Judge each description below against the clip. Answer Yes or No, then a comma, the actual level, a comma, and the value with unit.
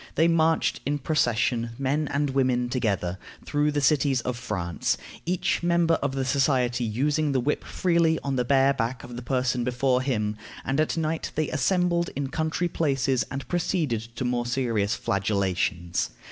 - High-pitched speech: No, low, 135 Hz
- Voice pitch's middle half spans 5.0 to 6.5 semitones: No, average, 4.0 semitones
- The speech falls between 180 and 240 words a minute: No, average, 165 wpm